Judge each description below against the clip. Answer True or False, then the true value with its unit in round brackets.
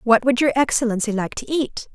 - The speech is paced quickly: True (215 wpm)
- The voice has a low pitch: False (245 Hz)